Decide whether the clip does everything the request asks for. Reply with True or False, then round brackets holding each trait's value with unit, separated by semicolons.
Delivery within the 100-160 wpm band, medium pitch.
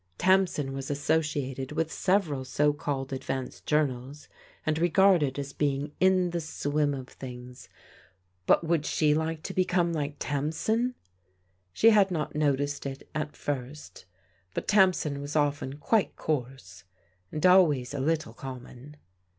True (140 wpm; 150 Hz)